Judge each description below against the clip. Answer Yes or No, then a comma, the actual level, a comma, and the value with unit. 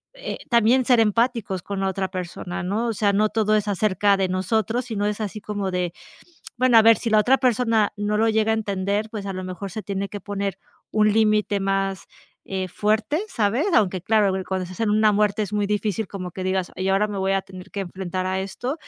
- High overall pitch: Yes, high, 205 Hz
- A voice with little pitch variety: Yes, narrow, 2.3 semitones